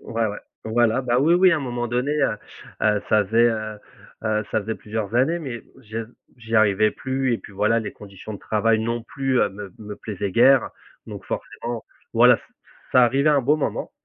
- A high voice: No, low, 115 Hz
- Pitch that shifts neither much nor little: Yes, average, 3.2 semitones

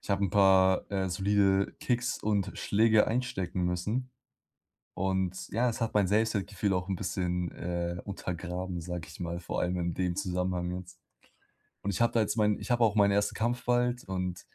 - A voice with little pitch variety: No, average, 3.1 semitones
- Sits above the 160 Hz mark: No, very low, 95 Hz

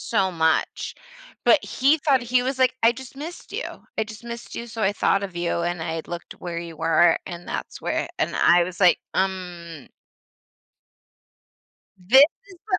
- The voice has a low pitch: No, high, 190 Hz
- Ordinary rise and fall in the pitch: No, wide, 6.3 semitones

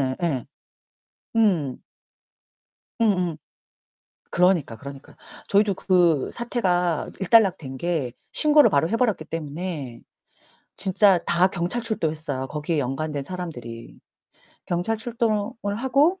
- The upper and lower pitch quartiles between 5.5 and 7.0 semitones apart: Yes, wide, 6.3 semitones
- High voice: No, medium, 175 Hz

